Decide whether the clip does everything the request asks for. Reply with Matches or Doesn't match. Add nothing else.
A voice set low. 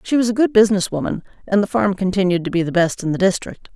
Doesn't match